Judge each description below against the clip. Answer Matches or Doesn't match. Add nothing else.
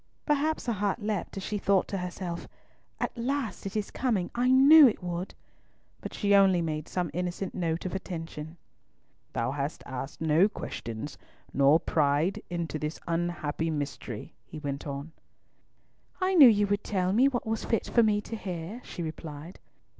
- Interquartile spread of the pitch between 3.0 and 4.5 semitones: Doesn't match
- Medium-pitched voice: Matches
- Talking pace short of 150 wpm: Doesn't match